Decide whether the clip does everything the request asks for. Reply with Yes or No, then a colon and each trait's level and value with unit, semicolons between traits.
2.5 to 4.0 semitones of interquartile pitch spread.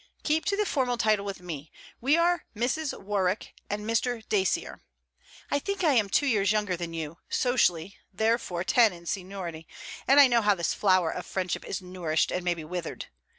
No: wide, 5.4 semitones